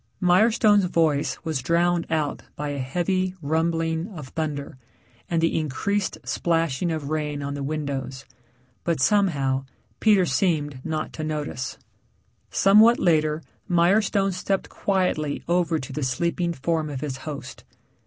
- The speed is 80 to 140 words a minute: Yes, slow, 135 wpm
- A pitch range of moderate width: Yes, average, 3.5 semitones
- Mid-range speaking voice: Yes, medium, 160 Hz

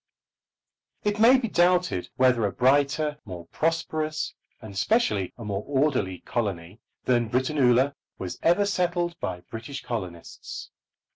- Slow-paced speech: Yes, slow, 125 wpm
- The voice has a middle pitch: No, low, 130 Hz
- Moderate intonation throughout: No, wide, 7.9 semitones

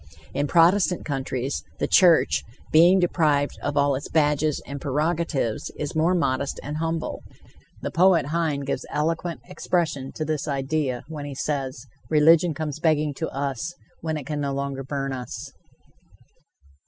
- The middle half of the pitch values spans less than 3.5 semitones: Yes, average, 2.8 semitones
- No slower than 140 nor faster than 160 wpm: Yes, average, 150 wpm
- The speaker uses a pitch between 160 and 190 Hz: No, medium, 150 Hz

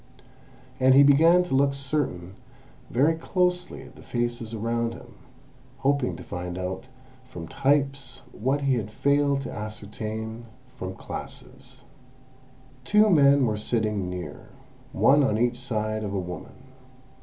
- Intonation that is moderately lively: Yes, average, 4.6 semitones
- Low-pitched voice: Yes, low, 120 Hz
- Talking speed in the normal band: No, slow, 130 wpm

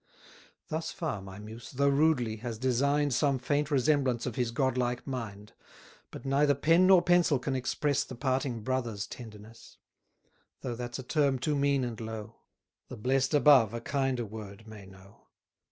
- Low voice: Yes, low, 130 Hz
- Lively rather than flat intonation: No, average, 3.9 semitones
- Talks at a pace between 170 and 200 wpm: No, average, 160 wpm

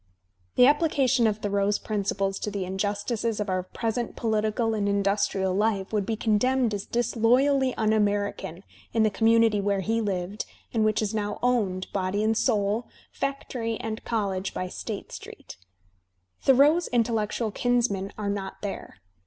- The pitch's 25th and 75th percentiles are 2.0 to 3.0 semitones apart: Yes, narrow, 2.5 semitones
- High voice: Yes, high, 215 Hz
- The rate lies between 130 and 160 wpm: Yes, average, 150 wpm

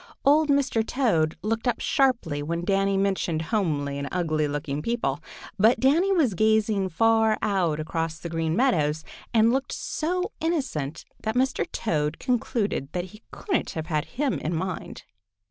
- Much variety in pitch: Yes, wide, 7.5 semitones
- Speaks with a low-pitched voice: No, high, 195 Hz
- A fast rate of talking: No, average, 155 wpm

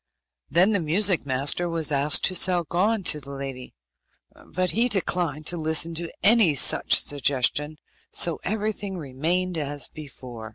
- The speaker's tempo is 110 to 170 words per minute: Yes, average, 150 wpm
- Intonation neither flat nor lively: Yes, average, 4.2 semitones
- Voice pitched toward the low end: No, medium, 165 Hz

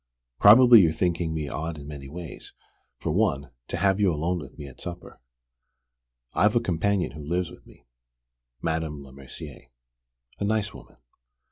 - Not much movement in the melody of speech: No, average, 4.5 semitones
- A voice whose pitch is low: Yes, very low, 80 Hz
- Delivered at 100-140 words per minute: No, average, 155 wpm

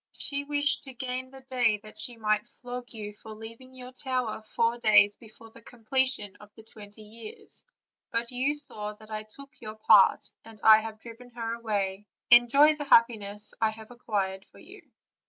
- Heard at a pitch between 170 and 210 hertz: No, high, 230 Hz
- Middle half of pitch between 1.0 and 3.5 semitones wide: Yes, average, 2.8 semitones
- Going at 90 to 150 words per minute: No, average, 185 wpm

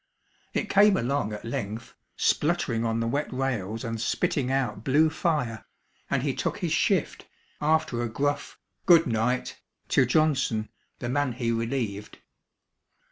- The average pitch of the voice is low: Yes, low, 125 Hz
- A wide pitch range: No, average, 4.0 semitones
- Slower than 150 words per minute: Yes, average, 140 wpm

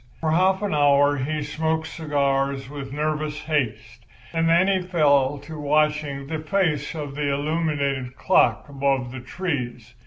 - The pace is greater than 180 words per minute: No, average, 150 wpm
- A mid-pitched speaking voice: Yes, medium, 145 Hz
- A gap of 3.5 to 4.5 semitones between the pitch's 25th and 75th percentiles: No, narrow, 2.5 semitones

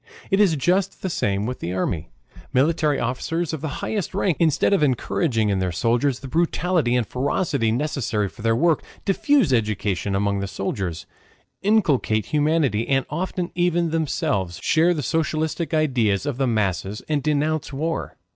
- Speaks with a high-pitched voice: No, medium, 140 Hz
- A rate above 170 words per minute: No, average, 160 wpm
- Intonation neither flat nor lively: No, wide, 7.0 semitones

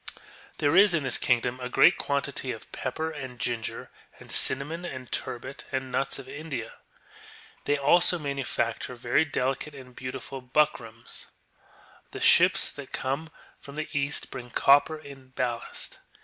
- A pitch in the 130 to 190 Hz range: Yes, low, 135 Hz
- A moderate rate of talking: Yes, average, 155 wpm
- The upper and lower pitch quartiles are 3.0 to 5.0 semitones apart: No, narrow, 2.5 semitones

